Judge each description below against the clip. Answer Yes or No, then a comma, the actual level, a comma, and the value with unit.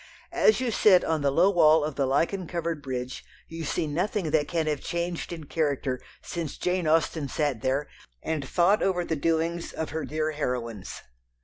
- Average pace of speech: Yes, average, 185 wpm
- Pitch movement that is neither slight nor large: Yes, average, 3.1 semitones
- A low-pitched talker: No, medium, 160 Hz